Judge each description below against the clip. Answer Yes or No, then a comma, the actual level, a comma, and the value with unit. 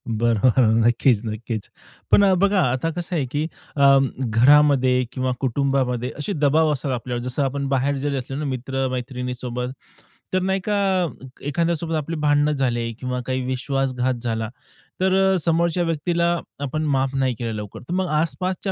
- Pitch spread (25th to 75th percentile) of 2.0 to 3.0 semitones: No, average, 3.7 semitones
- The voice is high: No, low, 135 Hz